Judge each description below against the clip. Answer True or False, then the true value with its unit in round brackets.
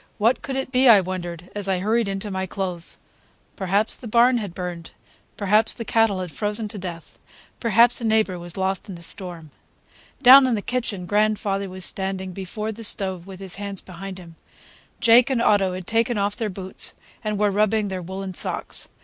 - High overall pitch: True (200 Hz)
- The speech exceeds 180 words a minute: True (190 wpm)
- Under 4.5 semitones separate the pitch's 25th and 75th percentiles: True (2.9 semitones)